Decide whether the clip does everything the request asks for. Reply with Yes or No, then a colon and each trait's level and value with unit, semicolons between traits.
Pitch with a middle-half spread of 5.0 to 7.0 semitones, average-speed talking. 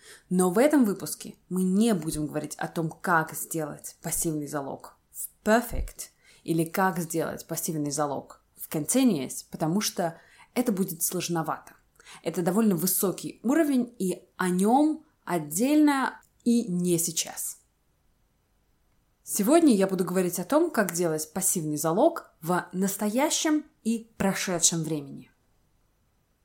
Yes: wide, 5.6 semitones; average, 120 wpm